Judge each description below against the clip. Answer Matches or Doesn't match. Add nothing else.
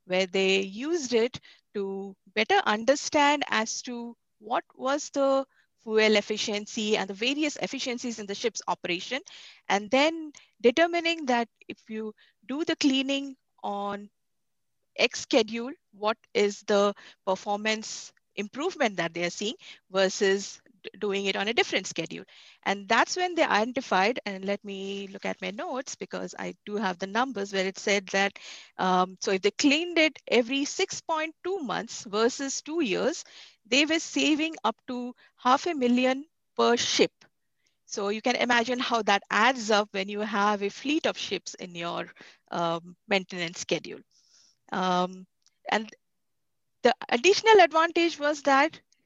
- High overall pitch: Matches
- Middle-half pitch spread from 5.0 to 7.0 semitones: Matches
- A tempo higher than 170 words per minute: Doesn't match